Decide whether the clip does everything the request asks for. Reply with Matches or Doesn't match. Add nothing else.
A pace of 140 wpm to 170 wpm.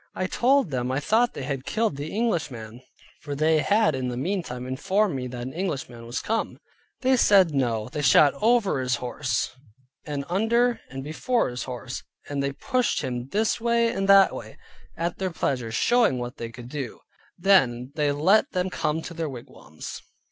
Doesn't match